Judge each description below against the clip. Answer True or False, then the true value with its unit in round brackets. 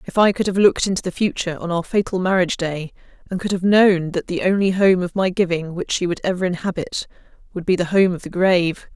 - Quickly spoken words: True (240 wpm)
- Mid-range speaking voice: True (180 Hz)